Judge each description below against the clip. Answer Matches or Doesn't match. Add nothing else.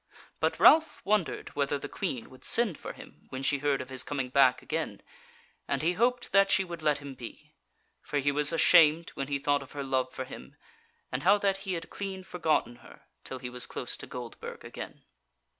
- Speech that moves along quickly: Matches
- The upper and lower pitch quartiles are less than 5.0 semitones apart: Doesn't match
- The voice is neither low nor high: Matches